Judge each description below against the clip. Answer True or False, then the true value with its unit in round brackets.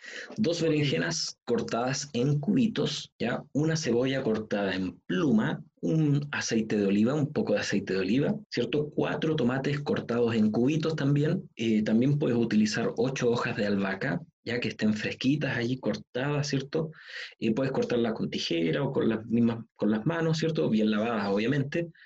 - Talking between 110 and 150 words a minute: False (165 wpm)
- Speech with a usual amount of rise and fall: False (5.9 semitones)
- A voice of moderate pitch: False (125 Hz)